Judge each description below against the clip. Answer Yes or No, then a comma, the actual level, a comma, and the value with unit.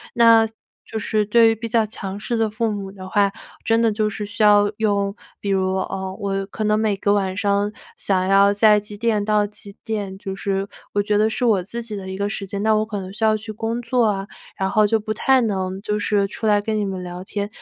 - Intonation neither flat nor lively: No, narrow, 1.8 semitones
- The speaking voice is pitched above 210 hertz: No, high, 205 Hz